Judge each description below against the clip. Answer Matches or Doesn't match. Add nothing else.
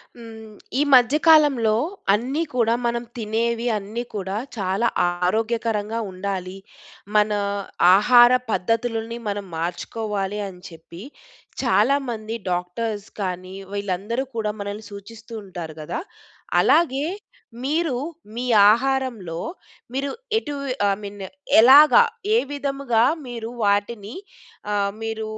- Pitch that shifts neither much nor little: Matches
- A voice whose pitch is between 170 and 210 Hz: Doesn't match